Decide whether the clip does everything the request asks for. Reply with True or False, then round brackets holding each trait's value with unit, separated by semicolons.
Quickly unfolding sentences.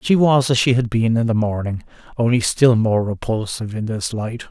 True (215 wpm)